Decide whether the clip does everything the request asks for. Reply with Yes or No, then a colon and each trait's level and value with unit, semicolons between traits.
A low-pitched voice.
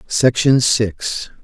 Yes: low, 120 Hz